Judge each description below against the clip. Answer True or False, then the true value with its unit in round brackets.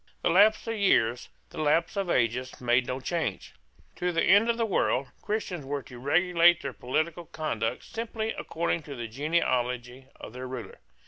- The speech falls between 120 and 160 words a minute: False (175 wpm)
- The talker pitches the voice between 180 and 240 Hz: False (155 Hz)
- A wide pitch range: True (6.1 semitones)